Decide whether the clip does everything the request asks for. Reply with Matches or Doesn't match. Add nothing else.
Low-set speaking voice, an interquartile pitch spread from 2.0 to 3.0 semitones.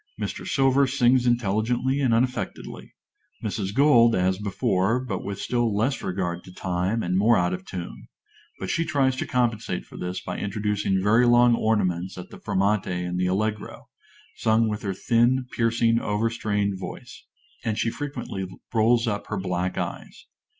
Doesn't match